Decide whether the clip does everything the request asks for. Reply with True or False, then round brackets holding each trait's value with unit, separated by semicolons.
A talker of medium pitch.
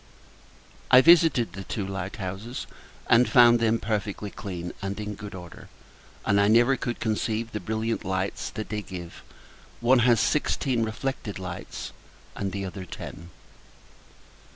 False (105 Hz)